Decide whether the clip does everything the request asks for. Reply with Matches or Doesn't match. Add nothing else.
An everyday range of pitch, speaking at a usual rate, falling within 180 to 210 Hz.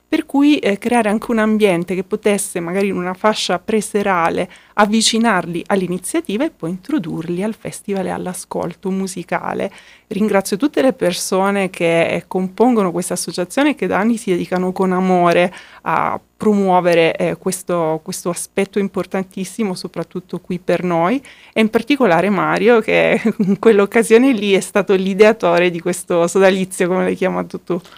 Matches